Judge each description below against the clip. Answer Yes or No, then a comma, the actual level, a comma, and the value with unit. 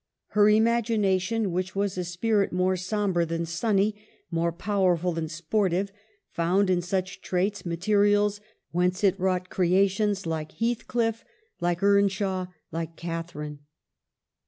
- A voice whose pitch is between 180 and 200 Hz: Yes, medium, 185 Hz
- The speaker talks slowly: Yes, slow, 125 wpm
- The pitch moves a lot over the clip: No, average, 2.9 semitones